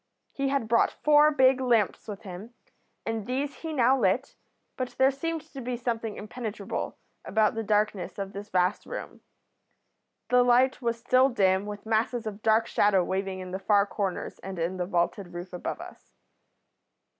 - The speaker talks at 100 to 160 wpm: No, average, 170 wpm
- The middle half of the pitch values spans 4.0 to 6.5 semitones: Yes, average, 4.4 semitones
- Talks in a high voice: Yes, high, 220 Hz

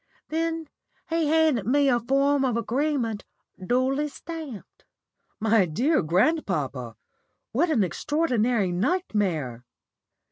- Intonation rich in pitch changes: Yes, wide, 7.3 semitones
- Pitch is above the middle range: Yes, very high, 250 Hz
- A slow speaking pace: Yes, slow, 100 wpm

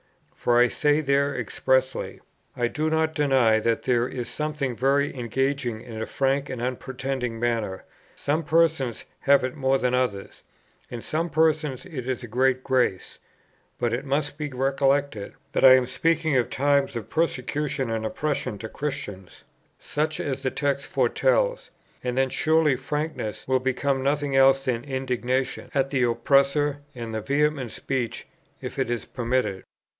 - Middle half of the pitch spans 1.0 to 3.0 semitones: Yes, average, 2.7 semitones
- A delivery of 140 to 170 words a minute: Yes, average, 155 wpm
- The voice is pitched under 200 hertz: Yes, low, 135 Hz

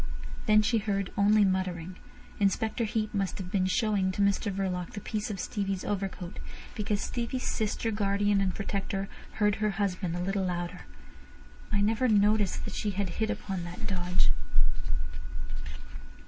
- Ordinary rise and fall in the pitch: No, narrow, 2.1 semitones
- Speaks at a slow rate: No, average, 150 wpm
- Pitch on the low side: No, high, 200 Hz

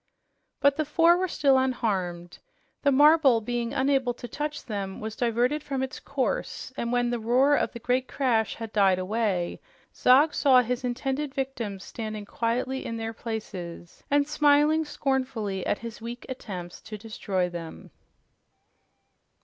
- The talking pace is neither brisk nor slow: Yes, average, 150 wpm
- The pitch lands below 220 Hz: No, high, 245 Hz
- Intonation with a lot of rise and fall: No, average, 4.1 semitones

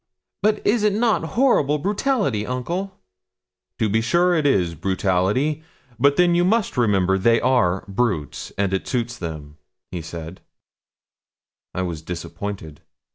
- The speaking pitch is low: Yes, low, 115 Hz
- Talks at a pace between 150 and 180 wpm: No, slow, 135 wpm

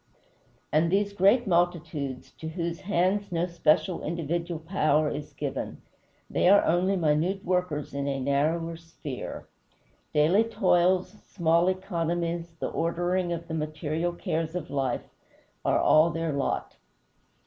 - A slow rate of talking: Yes, slow, 130 wpm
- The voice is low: No, medium, 170 Hz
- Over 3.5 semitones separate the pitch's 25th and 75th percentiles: No, narrow, 2.5 semitones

